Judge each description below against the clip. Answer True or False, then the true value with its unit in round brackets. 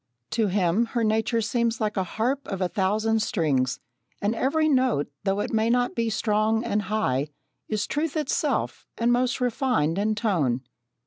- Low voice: False (220 Hz)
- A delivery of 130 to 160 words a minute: False (170 wpm)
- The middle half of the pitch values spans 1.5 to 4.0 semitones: True (3.5 semitones)